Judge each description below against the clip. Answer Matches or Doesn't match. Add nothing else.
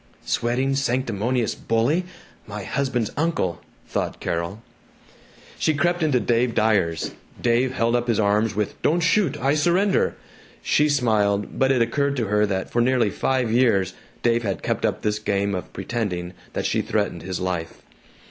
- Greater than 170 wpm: Doesn't match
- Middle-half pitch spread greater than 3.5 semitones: Matches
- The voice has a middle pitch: Doesn't match